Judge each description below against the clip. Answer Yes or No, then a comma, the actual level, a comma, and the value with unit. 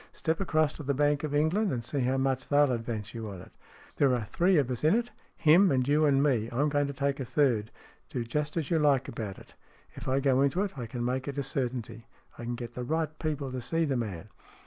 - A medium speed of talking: No, fast, 255 wpm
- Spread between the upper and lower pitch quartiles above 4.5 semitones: No, average, 3.7 semitones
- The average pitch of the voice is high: No, low, 135 Hz